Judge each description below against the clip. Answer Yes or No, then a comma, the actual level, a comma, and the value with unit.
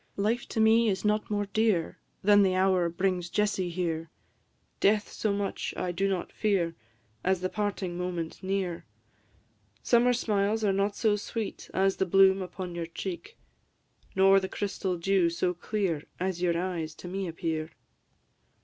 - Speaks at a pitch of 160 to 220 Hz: Yes, high, 190 Hz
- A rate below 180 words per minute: Yes, average, 160 wpm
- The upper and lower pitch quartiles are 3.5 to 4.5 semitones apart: No, narrow, 2.6 semitones